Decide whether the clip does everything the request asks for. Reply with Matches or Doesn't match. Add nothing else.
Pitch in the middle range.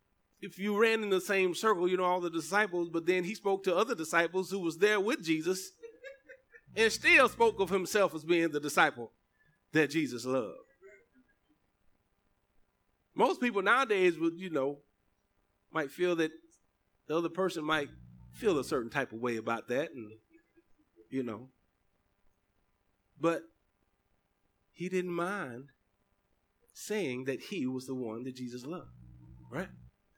Matches